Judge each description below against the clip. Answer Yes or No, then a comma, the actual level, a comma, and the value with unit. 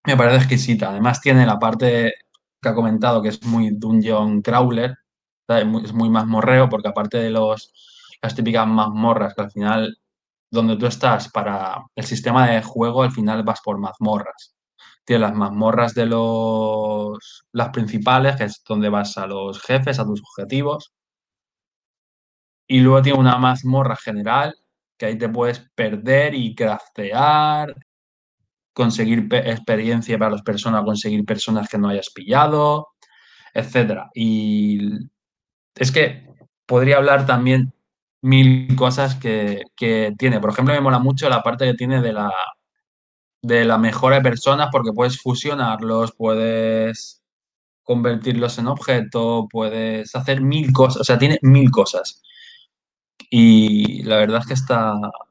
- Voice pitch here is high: No, low, 115 Hz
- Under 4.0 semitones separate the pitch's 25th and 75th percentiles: Yes, average, 2.9 semitones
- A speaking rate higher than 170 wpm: No, average, 145 wpm